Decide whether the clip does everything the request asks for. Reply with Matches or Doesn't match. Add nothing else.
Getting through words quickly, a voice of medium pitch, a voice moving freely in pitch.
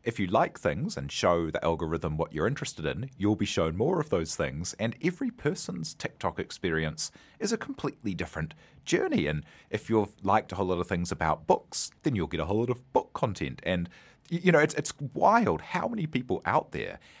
Doesn't match